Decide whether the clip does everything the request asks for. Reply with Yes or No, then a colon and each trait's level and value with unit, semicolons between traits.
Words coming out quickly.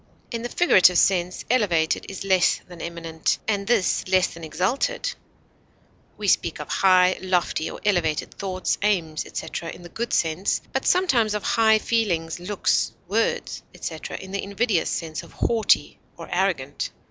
No: average, 155 wpm